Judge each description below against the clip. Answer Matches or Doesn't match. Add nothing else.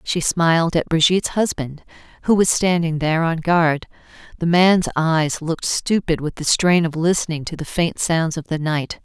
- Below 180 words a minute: Doesn't match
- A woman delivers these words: Matches